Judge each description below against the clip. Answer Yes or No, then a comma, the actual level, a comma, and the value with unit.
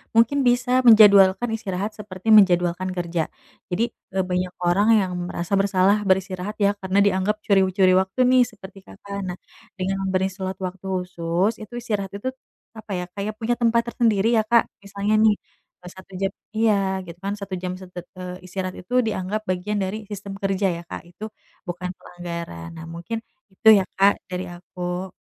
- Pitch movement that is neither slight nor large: No, narrow, 2.3 semitones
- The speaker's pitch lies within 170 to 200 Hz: Yes, high, 190 Hz